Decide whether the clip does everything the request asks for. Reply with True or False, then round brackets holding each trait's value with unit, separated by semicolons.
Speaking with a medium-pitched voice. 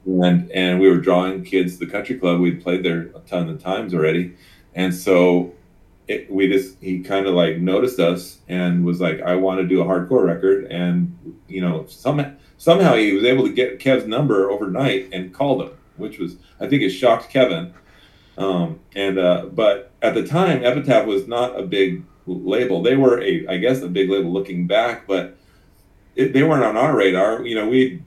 False (95 Hz)